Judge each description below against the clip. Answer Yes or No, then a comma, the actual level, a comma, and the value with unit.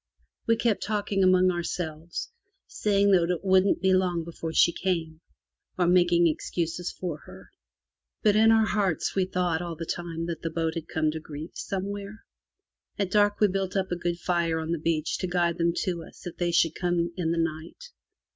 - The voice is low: No, medium, 175 Hz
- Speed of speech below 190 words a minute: No, average, 195 wpm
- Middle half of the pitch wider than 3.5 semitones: No, narrow, 2.5 semitones